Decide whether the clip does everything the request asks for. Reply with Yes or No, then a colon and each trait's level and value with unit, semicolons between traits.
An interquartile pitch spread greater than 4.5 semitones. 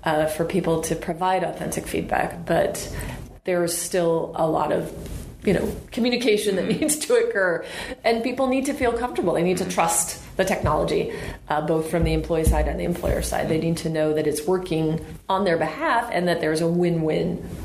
Yes: average, 5.1 semitones